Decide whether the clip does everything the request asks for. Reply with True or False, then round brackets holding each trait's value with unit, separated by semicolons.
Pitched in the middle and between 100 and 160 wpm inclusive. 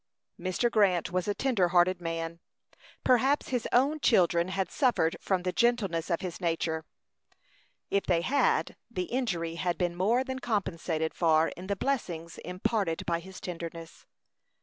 True (180 Hz; 150 wpm)